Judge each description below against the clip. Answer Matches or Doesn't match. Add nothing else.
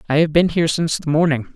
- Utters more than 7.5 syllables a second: Matches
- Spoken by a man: Matches